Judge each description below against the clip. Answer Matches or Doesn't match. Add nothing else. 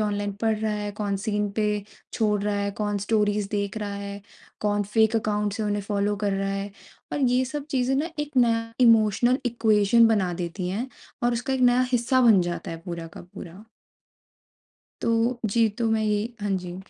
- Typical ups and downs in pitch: Doesn't match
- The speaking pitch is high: Matches